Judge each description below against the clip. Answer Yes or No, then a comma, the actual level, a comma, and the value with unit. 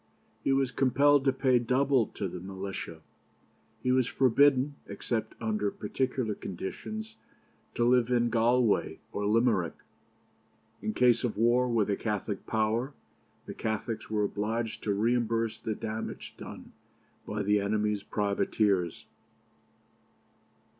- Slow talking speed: Yes, slow, 125 wpm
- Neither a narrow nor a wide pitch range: Yes, average, 3.3 semitones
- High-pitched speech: No, low, 115 Hz